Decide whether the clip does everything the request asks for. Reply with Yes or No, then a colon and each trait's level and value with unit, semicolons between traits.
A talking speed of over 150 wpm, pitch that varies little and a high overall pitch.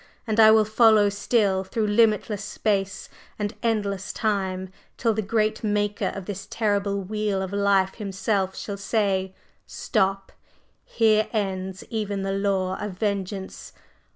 No: slow, 135 wpm; narrow, 1.9 semitones; high, 200 Hz